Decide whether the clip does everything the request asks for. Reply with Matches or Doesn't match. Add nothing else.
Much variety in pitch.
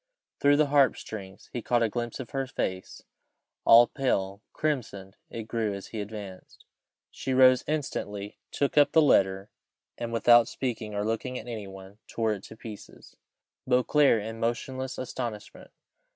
Doesn't match